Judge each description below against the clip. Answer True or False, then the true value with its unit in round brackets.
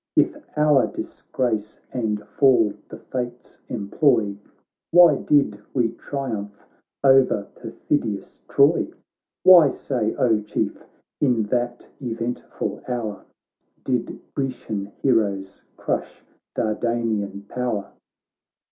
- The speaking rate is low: True (95 wpm)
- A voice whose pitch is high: False (120 Hz)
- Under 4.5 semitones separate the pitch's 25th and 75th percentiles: True (3.9 semitones)